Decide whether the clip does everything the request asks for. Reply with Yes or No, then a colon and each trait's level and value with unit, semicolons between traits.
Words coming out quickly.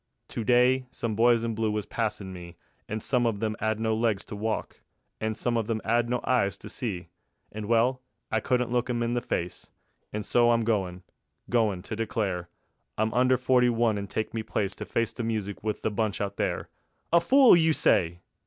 Yes: fast, 215 wpm